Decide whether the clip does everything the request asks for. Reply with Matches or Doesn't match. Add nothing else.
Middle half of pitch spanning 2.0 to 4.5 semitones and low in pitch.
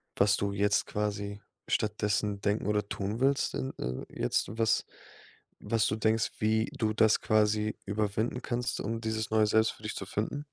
Doesn't match